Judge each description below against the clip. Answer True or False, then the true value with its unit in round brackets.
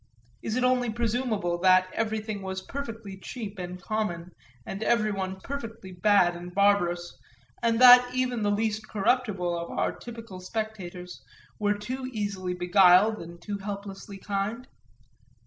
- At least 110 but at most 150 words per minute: True (135 wpm)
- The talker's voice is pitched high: True (205 Hz)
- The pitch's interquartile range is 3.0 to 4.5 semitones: True (3.4 semitones)